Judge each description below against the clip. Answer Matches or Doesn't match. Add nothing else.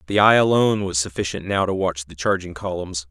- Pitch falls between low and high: Doesn't match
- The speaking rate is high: Matches